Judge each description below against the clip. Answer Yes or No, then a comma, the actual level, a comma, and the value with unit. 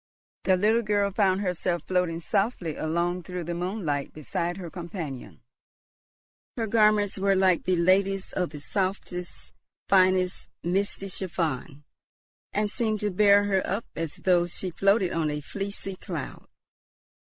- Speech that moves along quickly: No, average, 140 wpm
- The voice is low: No, medium, 185 Hz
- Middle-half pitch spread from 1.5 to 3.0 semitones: Yes, narrow, 2.6 semitones